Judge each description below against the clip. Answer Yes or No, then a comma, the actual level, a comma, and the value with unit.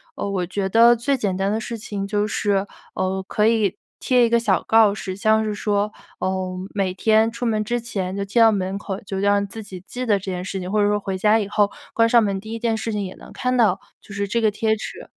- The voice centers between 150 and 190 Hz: No, high, 205 Hz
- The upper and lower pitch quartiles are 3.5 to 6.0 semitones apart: No, narrow, 2.5 semitones